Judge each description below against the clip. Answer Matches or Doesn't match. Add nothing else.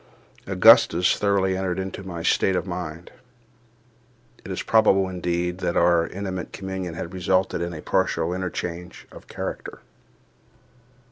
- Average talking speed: Doesn't match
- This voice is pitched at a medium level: Doesn't match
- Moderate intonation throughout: Doesn't match